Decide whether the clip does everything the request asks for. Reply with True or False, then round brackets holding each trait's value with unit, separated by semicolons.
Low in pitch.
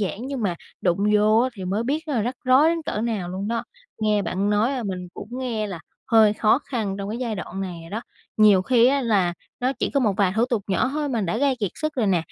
False (215 Hz)